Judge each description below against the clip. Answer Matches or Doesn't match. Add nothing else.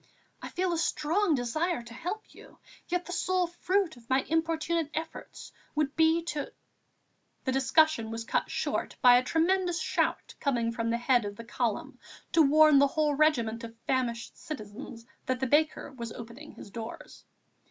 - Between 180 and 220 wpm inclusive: Doesn't match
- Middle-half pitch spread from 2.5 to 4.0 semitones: Doesn't match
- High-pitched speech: Matches